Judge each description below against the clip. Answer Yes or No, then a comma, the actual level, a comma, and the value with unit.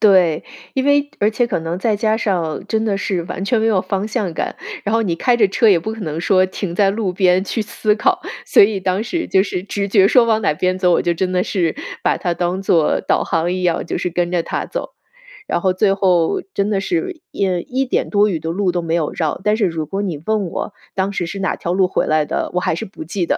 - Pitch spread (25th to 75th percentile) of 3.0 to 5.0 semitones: Yes, average, 3.6 semitones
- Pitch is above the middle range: Yes, high, 195 Hz